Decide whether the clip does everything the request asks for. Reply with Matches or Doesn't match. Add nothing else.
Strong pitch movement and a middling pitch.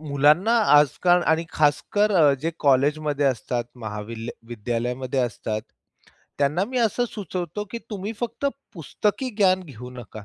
Matches